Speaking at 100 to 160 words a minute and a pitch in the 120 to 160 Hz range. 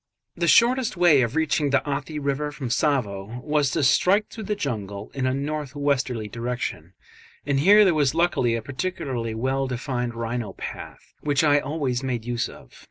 No: average, 175 wpm; low, 135 Hz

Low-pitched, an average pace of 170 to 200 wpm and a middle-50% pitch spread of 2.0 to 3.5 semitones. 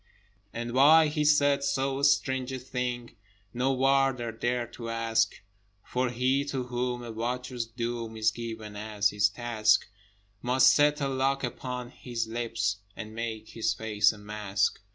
No: low, 120 Hz; average, 155 wpm; average, 2.8 semitones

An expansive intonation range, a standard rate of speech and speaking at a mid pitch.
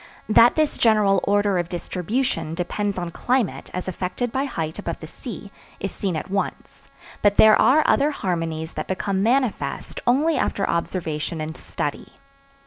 No: wide, 5.8 semitones; average, 155 wpm; high, 195 Hz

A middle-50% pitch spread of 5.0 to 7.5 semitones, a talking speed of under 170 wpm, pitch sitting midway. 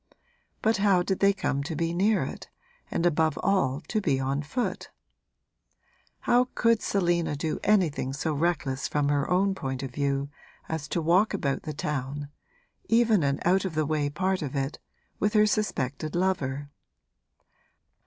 Yes: wide, 5.4 semitones; average, 160 wpm; medium, 160 Hz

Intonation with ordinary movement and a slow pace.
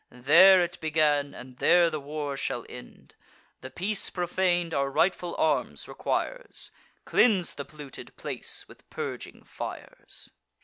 Yes: average, 3.9 semitones; slow, 130 wpm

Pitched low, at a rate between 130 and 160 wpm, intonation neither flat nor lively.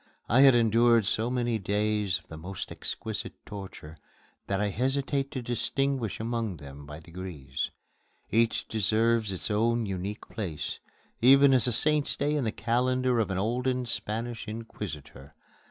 Yes: low, 115 Hz; average, 150 wpm; average, 4.1 semitones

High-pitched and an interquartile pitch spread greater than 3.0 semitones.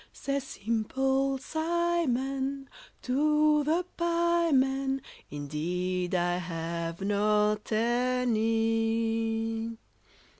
Yes: high, 235 Hz; average, 4.6 semitones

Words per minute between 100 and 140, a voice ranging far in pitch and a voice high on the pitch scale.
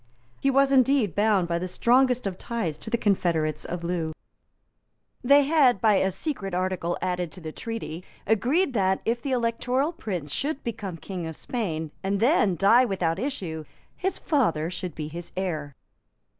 No: average, 165 wpm; wide, 6.4 semitones; high, 195 Hz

